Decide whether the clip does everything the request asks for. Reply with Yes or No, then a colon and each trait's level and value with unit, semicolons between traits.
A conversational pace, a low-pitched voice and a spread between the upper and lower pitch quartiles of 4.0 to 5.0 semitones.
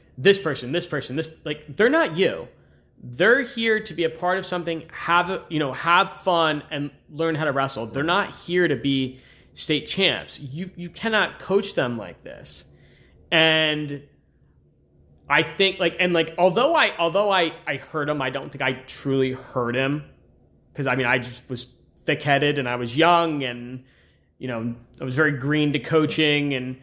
No: average, 185 wpm; medium, 150 Hz; average, 4.5 semitones